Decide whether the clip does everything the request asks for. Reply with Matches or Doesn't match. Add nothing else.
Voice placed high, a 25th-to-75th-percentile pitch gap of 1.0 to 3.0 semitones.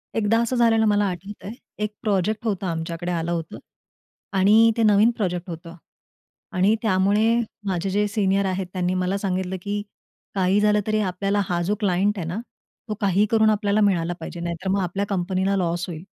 Matches